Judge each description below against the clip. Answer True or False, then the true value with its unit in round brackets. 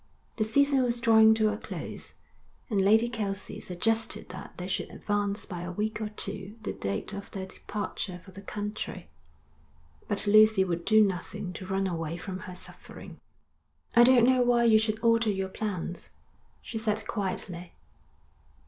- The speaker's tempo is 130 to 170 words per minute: True (165 wpm)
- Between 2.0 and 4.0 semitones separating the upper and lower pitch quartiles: True (2.6 semitones)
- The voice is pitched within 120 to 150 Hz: False (210 Hz)